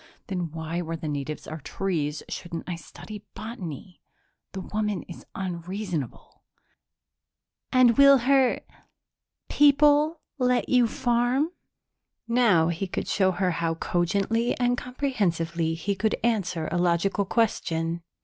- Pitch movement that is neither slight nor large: No, wide, 6.2 semitones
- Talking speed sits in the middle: No, slow, 120 wpm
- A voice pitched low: No, high, 190 Hz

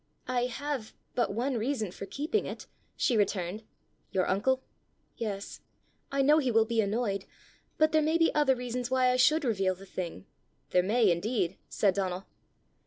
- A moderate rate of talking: Yes, average, 170 wpm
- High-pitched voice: Yes, high, 230 Hz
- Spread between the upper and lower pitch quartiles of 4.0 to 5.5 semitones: Yes, average, 5.1 semitones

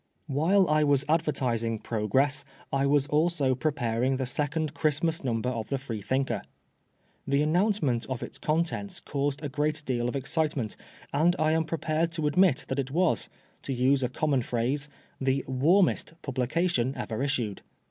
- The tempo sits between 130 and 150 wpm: No, average, 160 wpm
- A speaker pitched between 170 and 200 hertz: No, medium, 140 Hz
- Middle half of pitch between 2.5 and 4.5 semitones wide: Yes, average, 3.5 semitones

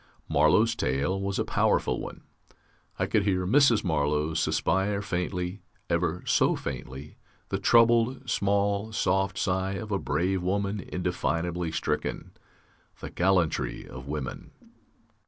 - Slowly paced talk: Yes, slow, 120 wpm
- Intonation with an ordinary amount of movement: Yes, average, 3.7 semitones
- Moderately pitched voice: No, very low, 95 Hz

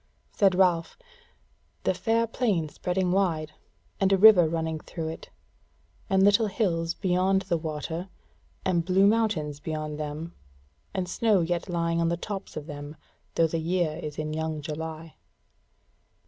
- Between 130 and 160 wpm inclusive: Yes, average, 145 wpm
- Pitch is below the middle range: No, medium, 170 Hz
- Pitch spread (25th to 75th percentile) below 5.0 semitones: Yes, average, 3.3 semitones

